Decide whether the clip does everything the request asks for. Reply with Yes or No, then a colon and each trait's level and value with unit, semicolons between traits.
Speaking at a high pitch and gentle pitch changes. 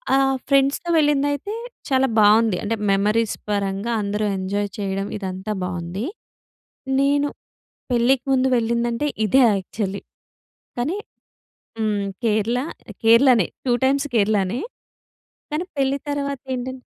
No: high, 230 Hz; average, 5.0 semitones